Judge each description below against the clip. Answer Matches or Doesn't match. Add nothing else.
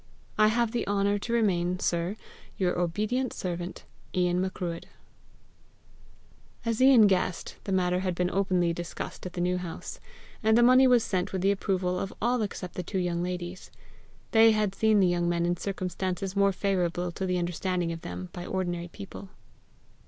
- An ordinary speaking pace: Matches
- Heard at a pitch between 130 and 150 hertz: Doesn't match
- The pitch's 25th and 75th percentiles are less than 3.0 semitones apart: Matches